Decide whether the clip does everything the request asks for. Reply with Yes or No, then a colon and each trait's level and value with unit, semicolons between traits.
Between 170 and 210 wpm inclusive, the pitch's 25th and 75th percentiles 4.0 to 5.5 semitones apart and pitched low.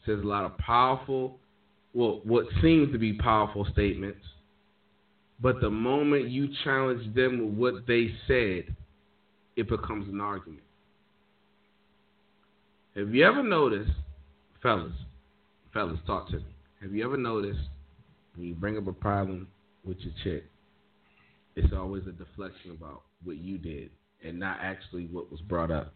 No: average, 145 wpm; average, 4.4 semitones; low, 100 Hz